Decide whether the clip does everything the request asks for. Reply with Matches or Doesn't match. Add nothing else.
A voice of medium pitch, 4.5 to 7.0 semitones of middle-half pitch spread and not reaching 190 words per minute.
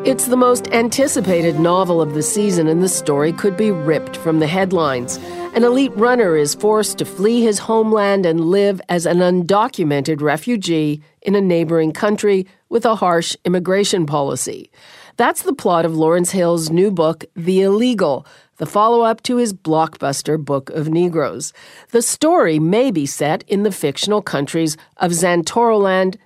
Matches